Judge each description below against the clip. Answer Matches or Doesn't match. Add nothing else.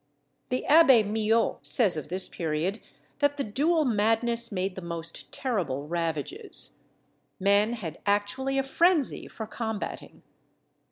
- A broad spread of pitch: Matches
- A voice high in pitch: Matches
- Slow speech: Matches